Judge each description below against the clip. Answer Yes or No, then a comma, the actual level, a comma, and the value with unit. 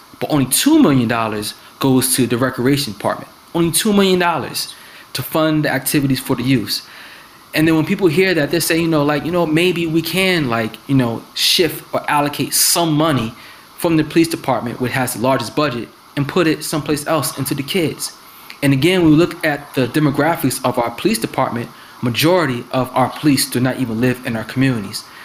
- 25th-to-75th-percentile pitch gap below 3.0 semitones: No, average, 4.3 semitones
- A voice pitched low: No, medium, 145 Hz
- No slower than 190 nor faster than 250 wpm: Yes, average, 195 wpm